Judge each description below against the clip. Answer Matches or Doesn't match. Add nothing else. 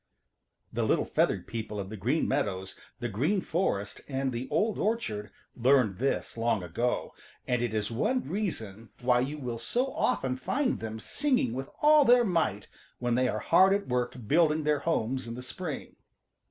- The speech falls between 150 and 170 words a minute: Doesn't match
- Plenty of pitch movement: Matches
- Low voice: Matches